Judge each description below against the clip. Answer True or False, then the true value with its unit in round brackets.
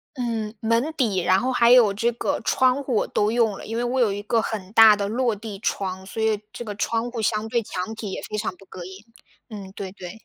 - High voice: True (220 Hz)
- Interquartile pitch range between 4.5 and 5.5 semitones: False (2.8 semitones)